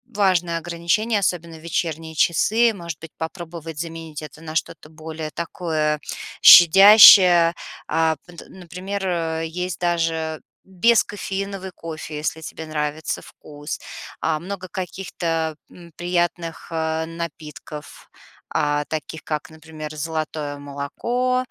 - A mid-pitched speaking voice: Yes, medium, 165 Hz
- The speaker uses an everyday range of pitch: No, narrow, 2.3 semitones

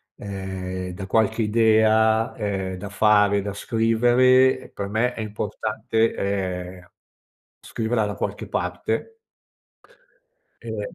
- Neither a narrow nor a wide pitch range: No, narrow, 2.3 semitones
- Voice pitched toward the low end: Yes, low, 110 Hz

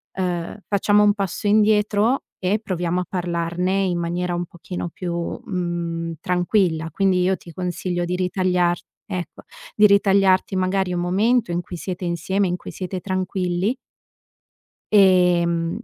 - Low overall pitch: No, medium, 180 Hz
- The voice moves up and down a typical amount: No, narrow, 2.0 semitones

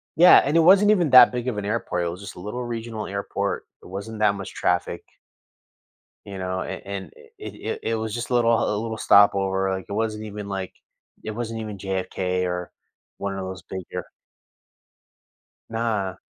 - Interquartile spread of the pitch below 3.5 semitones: Yes, average, 3.1 semitones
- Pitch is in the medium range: No, low, 100 Hz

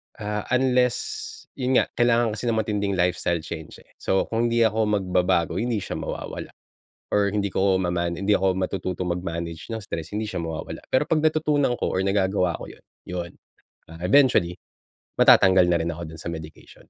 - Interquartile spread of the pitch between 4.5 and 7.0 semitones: Yes, average, 5.0 semitones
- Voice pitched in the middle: No, very low, 95 Hz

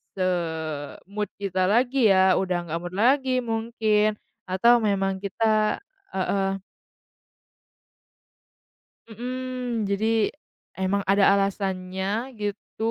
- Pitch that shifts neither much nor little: Yes, average, 3.1 semitones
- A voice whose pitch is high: Yes, high, 200 Hz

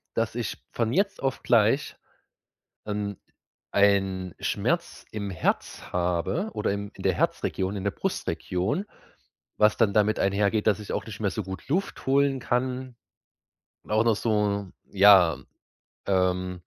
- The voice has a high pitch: No, low, 105 Hz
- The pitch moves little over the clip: No, average, 3.2 semitones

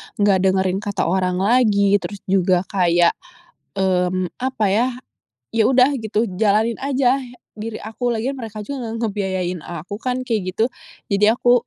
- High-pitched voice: Yes, high, 210 Hz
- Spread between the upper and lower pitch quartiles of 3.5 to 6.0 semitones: Yes, average, 3.8 semitones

